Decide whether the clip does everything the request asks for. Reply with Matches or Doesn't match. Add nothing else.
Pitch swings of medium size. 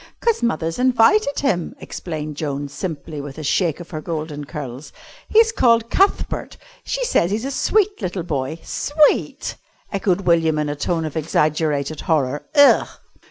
Doesn't match